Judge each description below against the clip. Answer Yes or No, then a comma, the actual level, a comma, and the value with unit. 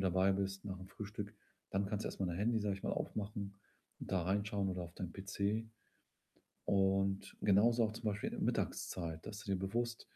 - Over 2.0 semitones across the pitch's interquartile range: No, narrow, 1.6 semitones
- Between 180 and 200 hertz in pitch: No, low, 100 Hz